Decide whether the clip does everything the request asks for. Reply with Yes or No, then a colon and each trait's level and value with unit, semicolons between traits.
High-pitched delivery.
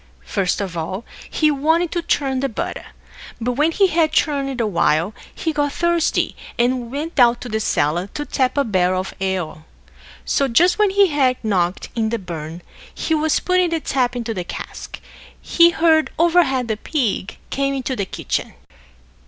Yes: very high, 260 Hz